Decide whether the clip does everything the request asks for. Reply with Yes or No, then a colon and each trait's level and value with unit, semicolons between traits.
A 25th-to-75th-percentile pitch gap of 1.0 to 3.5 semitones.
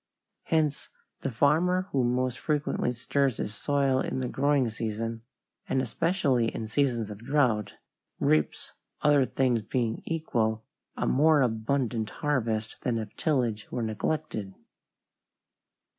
No: average, 4.3 semitones